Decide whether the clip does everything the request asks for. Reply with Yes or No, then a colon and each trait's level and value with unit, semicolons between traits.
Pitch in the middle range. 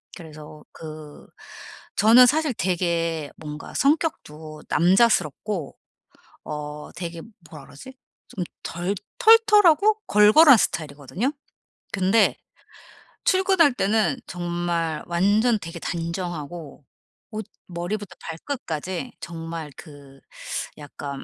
Yes: medium, 175 Hz